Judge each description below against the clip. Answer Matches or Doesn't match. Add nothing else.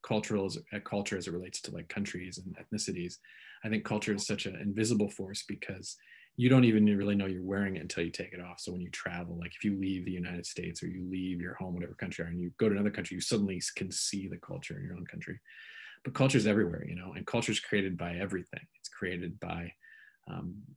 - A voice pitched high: Doesn't match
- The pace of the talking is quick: Matches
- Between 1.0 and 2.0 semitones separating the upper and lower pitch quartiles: Doesn't match